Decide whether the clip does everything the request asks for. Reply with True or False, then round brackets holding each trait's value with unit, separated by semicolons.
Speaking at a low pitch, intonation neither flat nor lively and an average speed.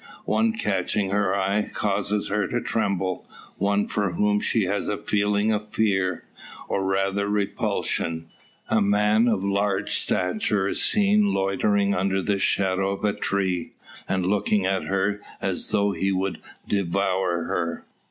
False (100 Hz; 1.4 semitones; 145 wpm)